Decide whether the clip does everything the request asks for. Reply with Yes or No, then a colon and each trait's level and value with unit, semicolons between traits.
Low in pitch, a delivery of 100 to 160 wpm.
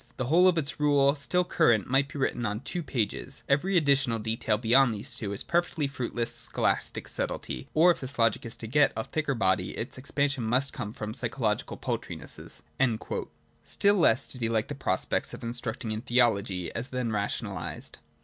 No: low, 125 Hz; average, 190 wpm